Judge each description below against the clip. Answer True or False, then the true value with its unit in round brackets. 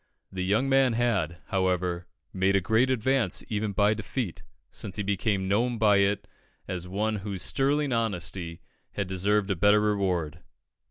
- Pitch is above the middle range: False (100 Hz)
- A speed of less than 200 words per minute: True (155 wpm)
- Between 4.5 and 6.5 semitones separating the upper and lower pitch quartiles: False (3.0 semitones)